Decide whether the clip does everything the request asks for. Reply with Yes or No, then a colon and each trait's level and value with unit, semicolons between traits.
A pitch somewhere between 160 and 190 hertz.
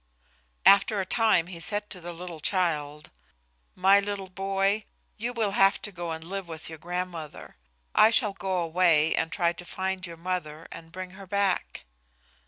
Yes: medium, 185 Hz